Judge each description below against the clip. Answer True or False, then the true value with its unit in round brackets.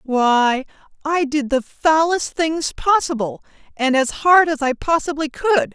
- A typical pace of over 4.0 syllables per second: False (3.9 syllables/s)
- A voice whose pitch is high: True (290 Hz)